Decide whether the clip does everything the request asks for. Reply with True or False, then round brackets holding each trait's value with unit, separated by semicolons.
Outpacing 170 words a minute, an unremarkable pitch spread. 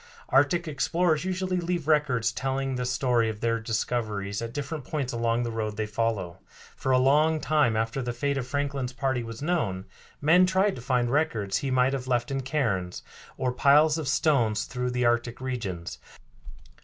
True (180 wpm; 4.1 semitones)